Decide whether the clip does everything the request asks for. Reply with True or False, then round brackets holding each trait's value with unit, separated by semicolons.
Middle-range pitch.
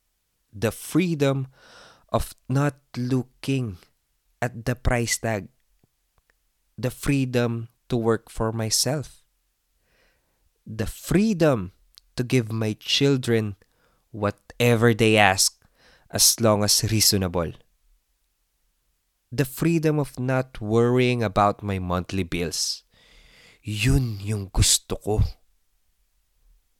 False (110 Hz)